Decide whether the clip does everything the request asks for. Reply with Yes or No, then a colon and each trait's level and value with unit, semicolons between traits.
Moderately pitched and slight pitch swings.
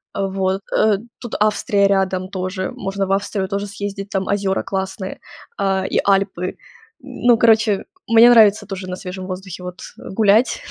No: high, 195 Hz; narrow, 1.4 semitones